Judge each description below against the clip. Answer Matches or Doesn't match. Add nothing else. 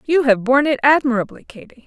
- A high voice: Matches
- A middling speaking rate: Matches